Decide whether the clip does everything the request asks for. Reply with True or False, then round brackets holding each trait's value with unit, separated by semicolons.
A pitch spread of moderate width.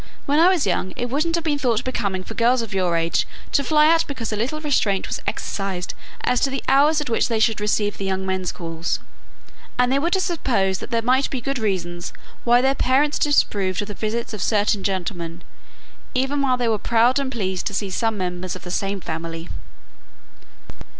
False (6.0 semitones)